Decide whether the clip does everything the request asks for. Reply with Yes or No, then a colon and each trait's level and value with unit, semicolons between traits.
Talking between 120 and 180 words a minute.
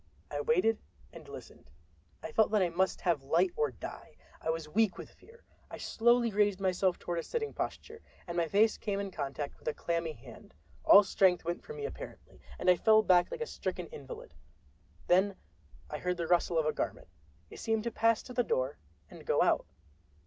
No: average, 200 wpm